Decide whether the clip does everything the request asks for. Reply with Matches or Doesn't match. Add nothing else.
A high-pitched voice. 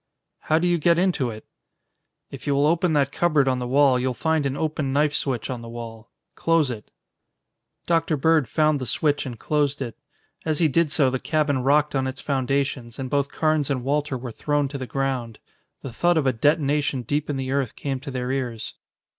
Doesn't match